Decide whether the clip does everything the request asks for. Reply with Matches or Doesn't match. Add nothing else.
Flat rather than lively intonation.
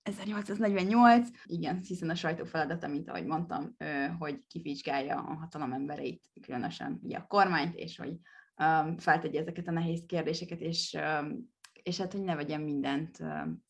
Doesn't match